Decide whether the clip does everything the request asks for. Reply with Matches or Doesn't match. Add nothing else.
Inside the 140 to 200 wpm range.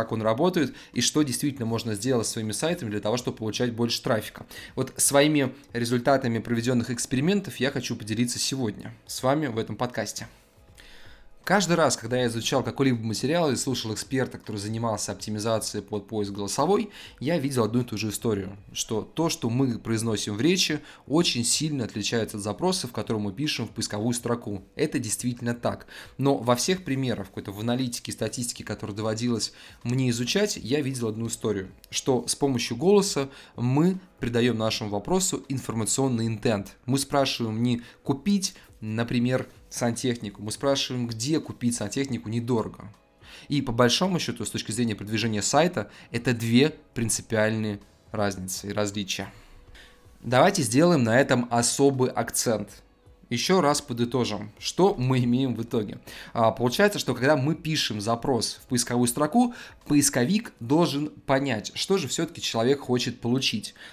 Matches